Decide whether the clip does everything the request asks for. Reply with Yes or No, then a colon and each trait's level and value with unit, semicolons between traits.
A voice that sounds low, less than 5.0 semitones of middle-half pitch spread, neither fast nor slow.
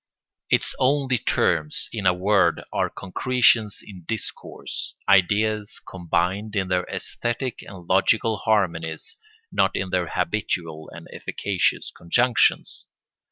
No: low, 100 Hz; average, 3.7 semitones; slow, 115 wpm